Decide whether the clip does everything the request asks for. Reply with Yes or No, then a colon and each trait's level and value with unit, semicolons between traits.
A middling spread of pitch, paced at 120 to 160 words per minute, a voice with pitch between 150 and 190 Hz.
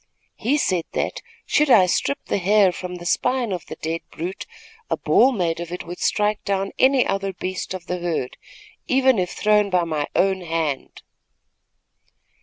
No: average, 3.5 semitones; average, 175 wpm; medium, 185 Hz